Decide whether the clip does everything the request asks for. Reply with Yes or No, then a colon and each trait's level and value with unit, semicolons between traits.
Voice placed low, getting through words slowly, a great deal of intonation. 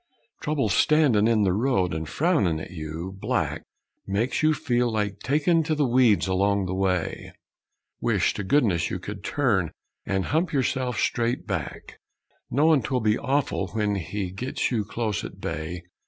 No: low, 110 Hz; average, 160 wpm; wide, 5.9 semitones